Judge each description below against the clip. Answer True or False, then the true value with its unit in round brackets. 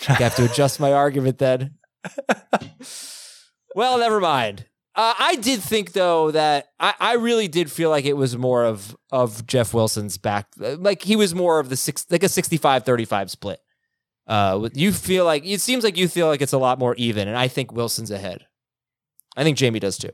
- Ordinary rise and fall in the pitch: False (7.1 semitones)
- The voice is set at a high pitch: False (140 Hz)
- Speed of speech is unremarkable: True (195 wpm)